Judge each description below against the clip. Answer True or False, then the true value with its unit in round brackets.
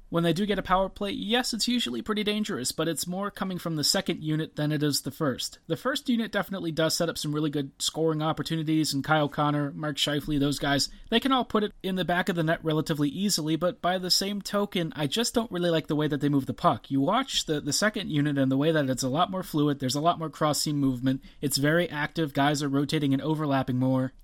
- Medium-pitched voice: True (160 Hz)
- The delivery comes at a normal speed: False (260 wpm)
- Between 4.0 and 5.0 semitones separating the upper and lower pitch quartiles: True (4.3 semitones)